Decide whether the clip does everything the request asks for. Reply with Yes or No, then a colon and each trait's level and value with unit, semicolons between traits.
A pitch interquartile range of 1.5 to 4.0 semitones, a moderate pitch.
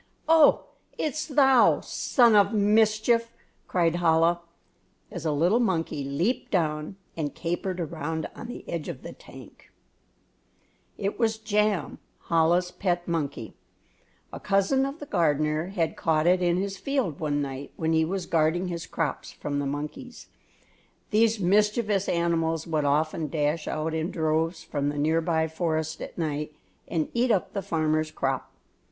No: average, 4.6 semitones; medium, 170 Hz